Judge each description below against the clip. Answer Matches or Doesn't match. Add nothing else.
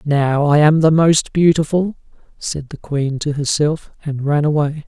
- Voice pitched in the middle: Matches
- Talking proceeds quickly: Doesn't match